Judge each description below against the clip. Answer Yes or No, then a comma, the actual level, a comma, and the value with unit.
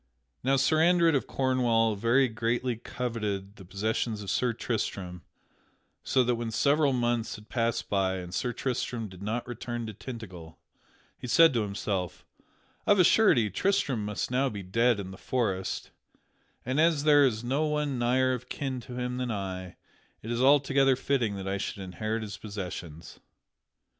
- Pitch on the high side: No, low, 115 Hz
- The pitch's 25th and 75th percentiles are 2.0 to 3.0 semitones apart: No, average, 4.3 semitones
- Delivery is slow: No, average, 170 wpm